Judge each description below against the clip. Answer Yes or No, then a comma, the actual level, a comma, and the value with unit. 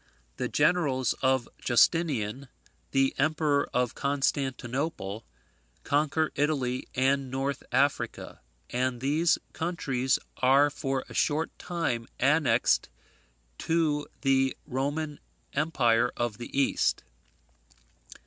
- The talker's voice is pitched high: No, low, 135 Hz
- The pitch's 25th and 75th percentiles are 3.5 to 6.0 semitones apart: No, average, 2.7 semitones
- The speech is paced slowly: Yes, slow, 95 wpm